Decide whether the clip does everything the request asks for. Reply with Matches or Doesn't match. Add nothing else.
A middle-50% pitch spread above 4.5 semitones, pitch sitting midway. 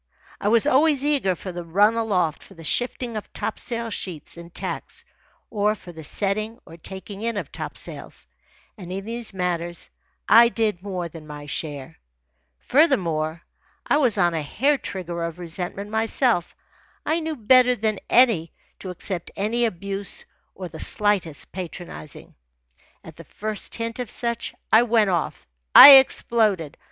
Doesn't match